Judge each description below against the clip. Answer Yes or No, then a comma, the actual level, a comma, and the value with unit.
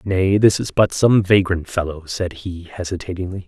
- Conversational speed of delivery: Yes, average, 175 wpm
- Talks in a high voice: No, very low, 90 Hz